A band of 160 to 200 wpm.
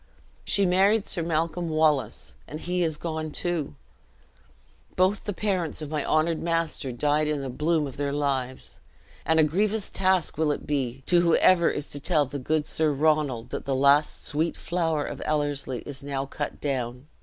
Yes: average, 180 wpm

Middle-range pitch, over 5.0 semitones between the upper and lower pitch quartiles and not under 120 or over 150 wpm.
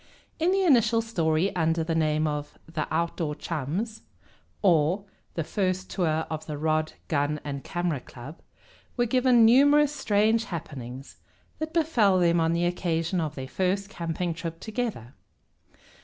Yes: medium, 170 Hz; wide, 5.6 semitones; average, 145 wpm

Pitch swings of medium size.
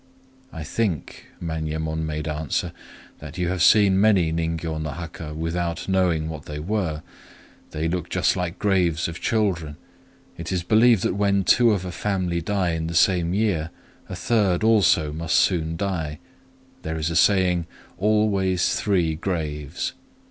Yes: average, 3.3 semitones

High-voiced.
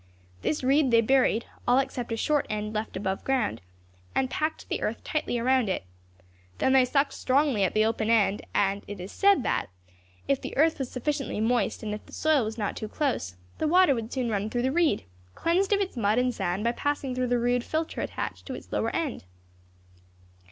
Yes: high, 245 Hz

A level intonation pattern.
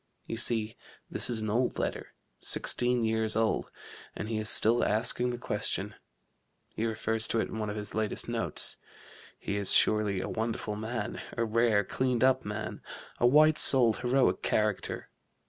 Yes: narrow, 2.1 semitones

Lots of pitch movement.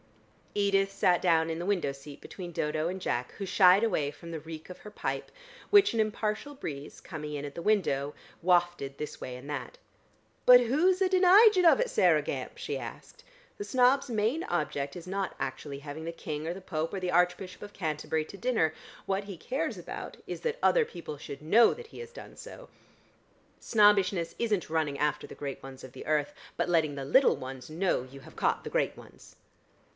Yes: wide, 6.3 semitones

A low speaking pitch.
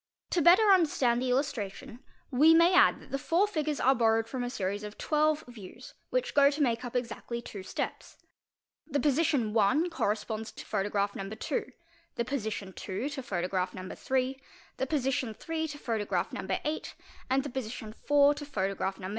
No: very high, 250 Hz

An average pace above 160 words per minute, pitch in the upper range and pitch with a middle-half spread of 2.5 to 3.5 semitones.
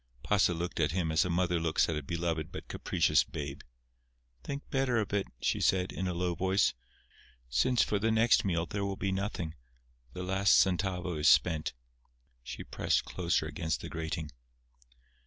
No: average, 175 wpm; very low, 90 Hz; average, 3.2 semitones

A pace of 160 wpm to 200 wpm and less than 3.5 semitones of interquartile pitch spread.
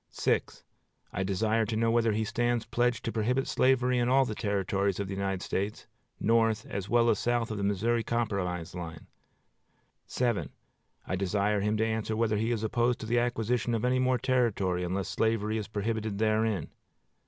Yes: average, 175 wpm; average, 2.9 semitones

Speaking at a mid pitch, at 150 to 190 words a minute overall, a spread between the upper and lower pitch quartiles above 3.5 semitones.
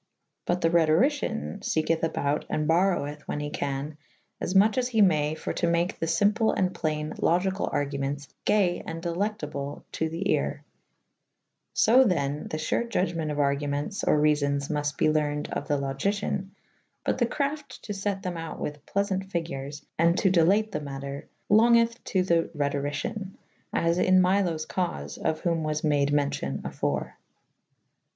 Yes: medium, 165 Hz; average, 160 wpm; average, 4.7 semitones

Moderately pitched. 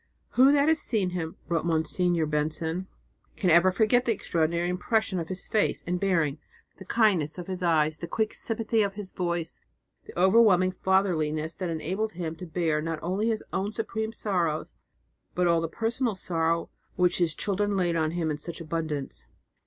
Yes: medium, 180 Hz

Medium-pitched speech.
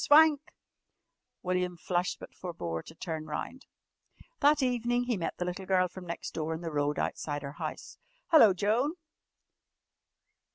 Yes: medium, 180 Hz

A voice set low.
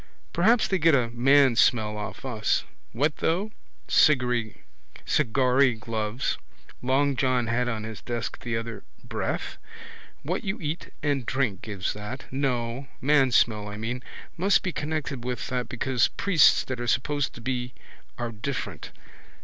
Yes: low, 125 Hz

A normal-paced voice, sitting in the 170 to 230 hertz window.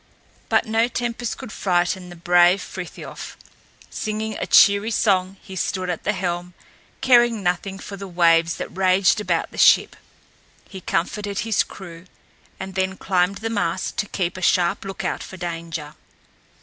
Yes: average, 155 wpm; high, 190 Hz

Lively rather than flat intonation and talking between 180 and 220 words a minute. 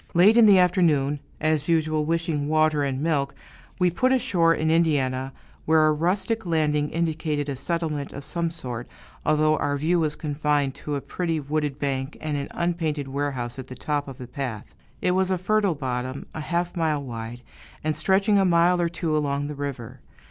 No: average, 3.2 semitones; average, 185 wpm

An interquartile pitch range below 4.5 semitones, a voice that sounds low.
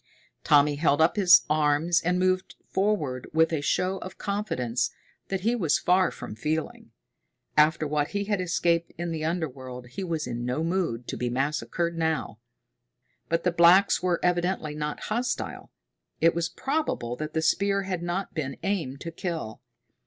No: average, 3.7 semitones; medium, 165 Hz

